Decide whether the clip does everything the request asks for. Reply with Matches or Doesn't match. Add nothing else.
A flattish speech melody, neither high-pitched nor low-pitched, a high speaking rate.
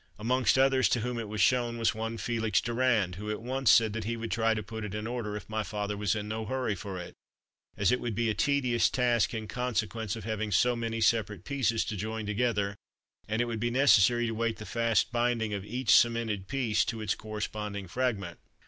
Doesn't match